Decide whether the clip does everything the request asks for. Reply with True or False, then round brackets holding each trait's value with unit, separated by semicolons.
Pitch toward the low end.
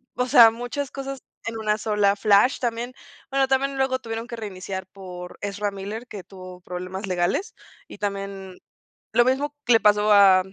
False (210 Hz)